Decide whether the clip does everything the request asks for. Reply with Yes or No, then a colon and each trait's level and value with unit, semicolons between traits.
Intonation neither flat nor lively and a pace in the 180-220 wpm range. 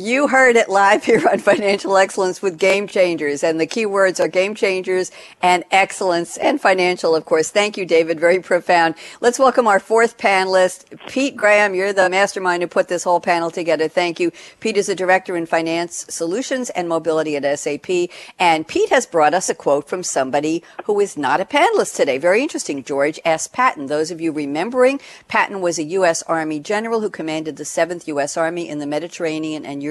Yes: average, 3.8 semitones; average, 200 wpm